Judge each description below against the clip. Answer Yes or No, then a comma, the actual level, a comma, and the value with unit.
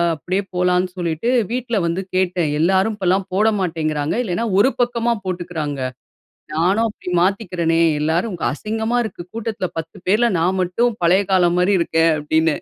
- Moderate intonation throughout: Yes, average, 4.2 semitones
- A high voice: No, medium, 180 Hz